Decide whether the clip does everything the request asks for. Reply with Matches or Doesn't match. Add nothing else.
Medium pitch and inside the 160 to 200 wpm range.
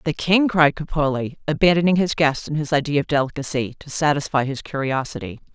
Matches